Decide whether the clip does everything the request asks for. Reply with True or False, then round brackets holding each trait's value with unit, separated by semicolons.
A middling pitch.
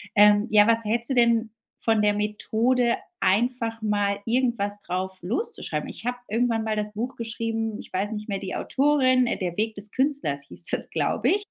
False (225 Hz)